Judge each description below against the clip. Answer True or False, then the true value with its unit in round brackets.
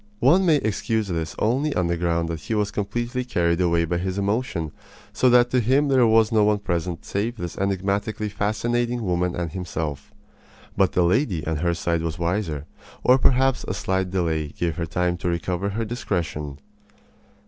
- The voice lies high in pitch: False (95 Hz)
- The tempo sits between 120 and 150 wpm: False (180 wpm)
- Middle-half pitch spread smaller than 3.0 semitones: False (5.0 semitones)